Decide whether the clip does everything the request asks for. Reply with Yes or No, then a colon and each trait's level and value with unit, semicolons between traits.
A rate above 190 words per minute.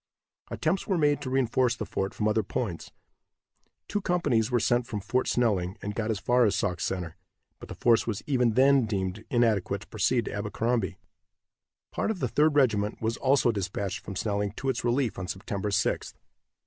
No: average, 185 wpm